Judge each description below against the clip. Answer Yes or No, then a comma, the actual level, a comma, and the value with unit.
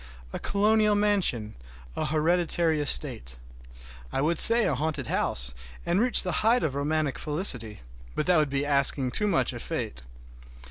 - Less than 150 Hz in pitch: No, medium, 155 Hz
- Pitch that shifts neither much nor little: No, wide, 6.1 semitones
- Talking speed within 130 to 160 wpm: Yes, average, 150 wpm